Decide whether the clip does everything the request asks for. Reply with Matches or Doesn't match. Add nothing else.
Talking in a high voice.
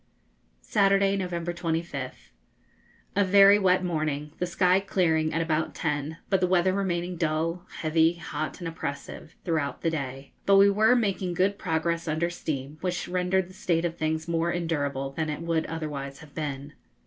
Doesn't match